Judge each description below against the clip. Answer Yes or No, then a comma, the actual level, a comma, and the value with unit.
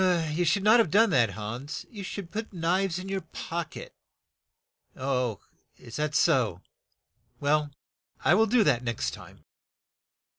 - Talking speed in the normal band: Yes, average, 150 wpm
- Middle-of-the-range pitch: Yes, medium, 165 Hz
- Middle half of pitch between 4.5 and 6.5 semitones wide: Yes, wide, 5.5 semitones